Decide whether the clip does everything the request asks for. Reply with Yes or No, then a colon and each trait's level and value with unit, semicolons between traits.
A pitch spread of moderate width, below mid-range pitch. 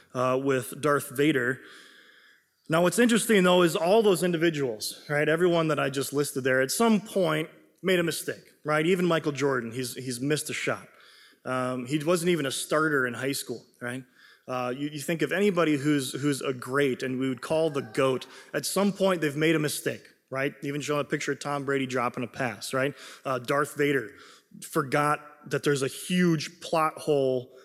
No: average, 4.1 semitones; medium, 145 Hz